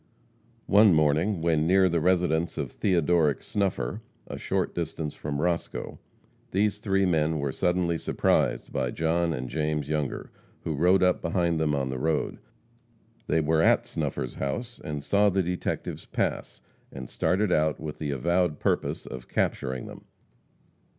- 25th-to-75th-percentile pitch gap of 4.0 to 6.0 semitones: No, average, 3.4 semitones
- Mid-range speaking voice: No, very low, 80 Hz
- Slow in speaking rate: No, average, 150 wpm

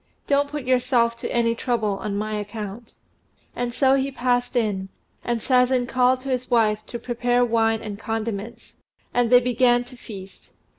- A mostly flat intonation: Yes, narrow, 2.2 semitones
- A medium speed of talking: Yes, average, 165 wpm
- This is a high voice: Yes, high, 240 Hz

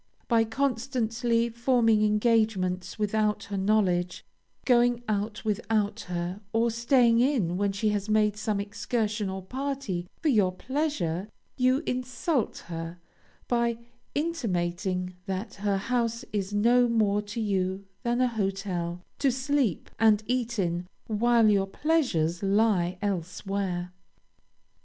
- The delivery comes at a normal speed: No, slow, 125 wpm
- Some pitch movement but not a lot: Yes, average, 3.7 semitones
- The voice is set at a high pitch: Yes, high, 215 Hz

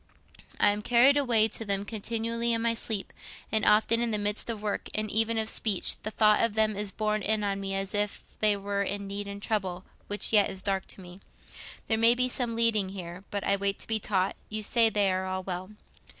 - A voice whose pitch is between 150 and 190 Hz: No, high, 210 Hz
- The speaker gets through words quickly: Yes, fast, 230 wpm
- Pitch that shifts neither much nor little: No, narrow, 2.1 semitones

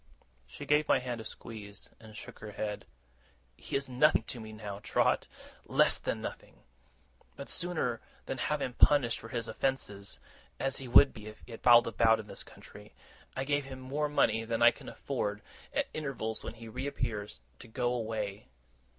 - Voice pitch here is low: Yes, low, 115 Hz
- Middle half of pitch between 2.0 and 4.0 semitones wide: Yes, average, 3.7 semitones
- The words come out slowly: No, average, 180 wpm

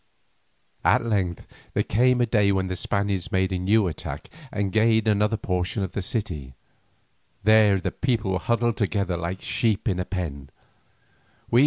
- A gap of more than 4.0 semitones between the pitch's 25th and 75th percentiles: No, average, 3.1 semitones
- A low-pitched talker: Yes, low, 100 Hz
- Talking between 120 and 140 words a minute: No, average, 160 wpm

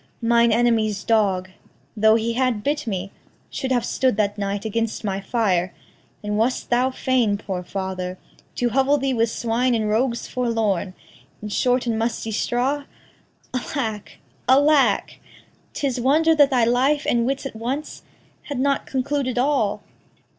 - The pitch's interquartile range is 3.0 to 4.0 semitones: Yes, average, 3.7 semitones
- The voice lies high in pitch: Yes, high, 235 Hz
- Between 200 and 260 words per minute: No, average, 145 wpm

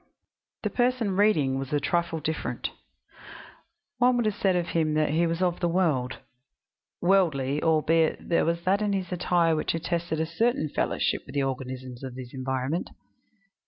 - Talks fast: No, average, 165 wpm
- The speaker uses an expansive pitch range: No, average, 4.6 semitones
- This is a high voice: No, medium, 165 Hz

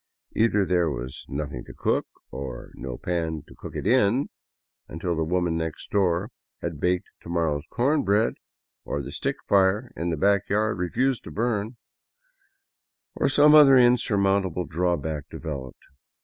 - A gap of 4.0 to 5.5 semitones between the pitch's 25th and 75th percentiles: Yes, average, 5.2 semitones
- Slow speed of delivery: No, average, 155 wpm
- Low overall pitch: Yes, very low, 90 Hz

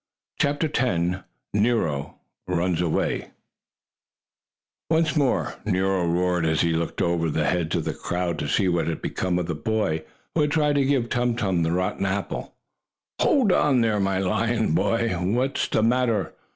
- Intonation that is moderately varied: No, wide, 6.0 semitones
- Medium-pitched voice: No, very low, 95 Hz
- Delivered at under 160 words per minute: No, average, 165 wpm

